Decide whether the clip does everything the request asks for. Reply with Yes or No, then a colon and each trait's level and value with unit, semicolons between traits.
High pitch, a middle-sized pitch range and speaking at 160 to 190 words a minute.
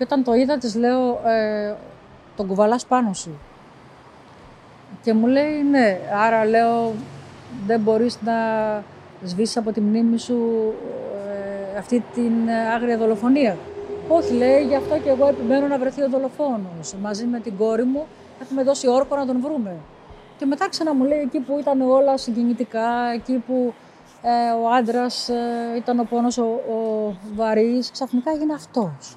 No: high, 235 Hz; average, 3.2 semitones; average, 145 wpm